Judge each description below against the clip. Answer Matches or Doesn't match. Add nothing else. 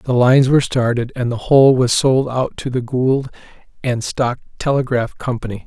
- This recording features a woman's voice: Doesn't match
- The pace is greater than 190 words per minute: Doesn't match